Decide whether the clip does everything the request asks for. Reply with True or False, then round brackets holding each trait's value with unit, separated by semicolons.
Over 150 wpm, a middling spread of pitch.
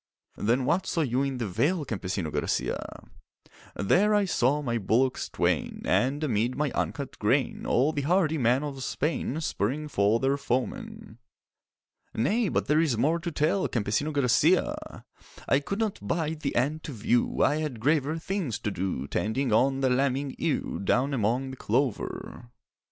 True (160 wpm; 4.4 semitones)